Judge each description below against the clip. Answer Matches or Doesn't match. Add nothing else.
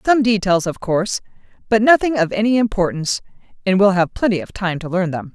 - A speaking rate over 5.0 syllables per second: Matches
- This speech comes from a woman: Matches